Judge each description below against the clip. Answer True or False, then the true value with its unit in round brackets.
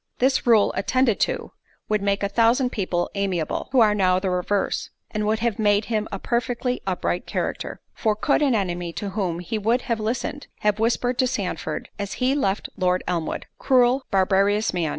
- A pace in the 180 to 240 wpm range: True (185 wpm)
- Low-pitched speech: False (210 Hz)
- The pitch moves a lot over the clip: False (4.1 semitones)